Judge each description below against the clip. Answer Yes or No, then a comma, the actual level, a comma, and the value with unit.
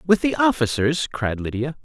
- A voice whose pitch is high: No, low, 135 Hz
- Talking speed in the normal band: Yes, average, 165 wpm